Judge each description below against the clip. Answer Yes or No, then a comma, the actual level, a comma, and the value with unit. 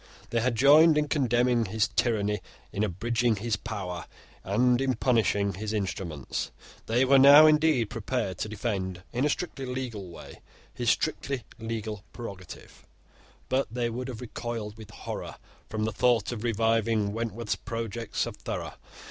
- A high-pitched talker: No, low, 115 Hz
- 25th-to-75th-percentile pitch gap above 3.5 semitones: No, average, 3.1 semitones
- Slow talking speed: No, average, 150 wpm